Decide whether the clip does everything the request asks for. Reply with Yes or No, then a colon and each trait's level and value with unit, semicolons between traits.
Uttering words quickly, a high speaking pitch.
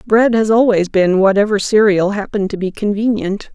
No: average, 170 wpm; high, 205 Hz